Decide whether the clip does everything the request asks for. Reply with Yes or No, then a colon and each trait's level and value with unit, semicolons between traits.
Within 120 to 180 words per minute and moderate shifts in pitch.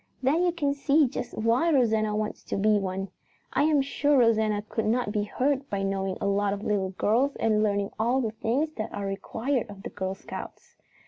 No: fast, 205 wpm; average, 4.8 semitones